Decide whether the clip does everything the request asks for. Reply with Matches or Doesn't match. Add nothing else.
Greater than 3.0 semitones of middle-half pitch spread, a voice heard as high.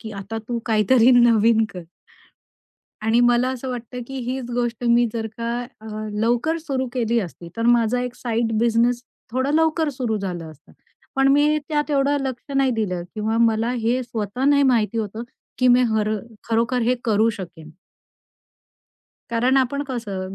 Doesn't match